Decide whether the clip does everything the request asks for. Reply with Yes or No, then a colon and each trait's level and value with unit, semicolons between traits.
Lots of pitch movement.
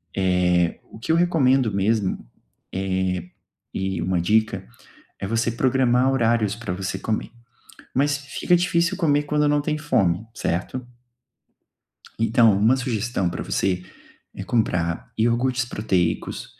Yes: wide, 5.8 semitones